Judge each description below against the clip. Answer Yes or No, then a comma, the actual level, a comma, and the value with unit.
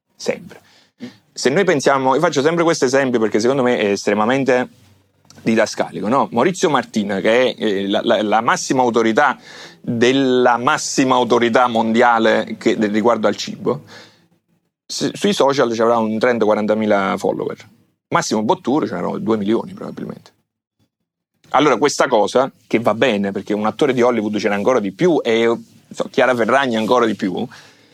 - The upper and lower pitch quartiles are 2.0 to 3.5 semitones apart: Yes, average, 2.8 semitones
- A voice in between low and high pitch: No, low, 115 Hz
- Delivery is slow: No, average, 150 wpm